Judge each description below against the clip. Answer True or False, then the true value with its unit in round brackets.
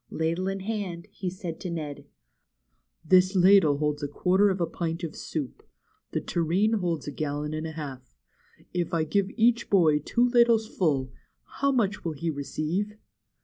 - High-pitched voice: False (170 Hz)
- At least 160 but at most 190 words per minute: True (170 wpm)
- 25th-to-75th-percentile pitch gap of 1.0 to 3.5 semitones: False (4.4 semitones)